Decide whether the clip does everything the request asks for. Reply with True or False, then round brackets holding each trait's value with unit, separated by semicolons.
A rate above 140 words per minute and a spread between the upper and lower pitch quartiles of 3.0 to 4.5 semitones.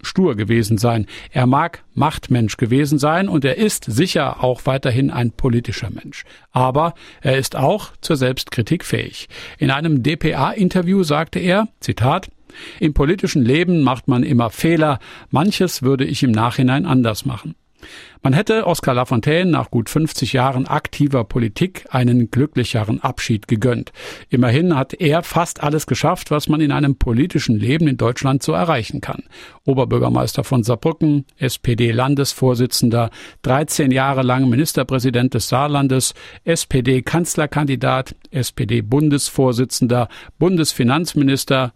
False (130 wpm; 3.7 semitones)